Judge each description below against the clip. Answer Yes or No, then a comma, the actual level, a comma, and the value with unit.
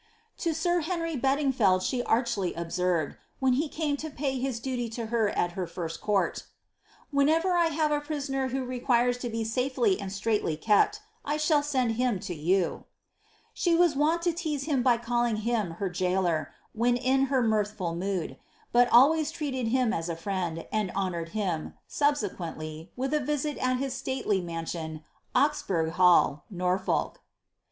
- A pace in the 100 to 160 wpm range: No, average, 175 wpm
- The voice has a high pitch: Yes, high, 240 Hz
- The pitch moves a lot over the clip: Yes, wide, 7.3 semitones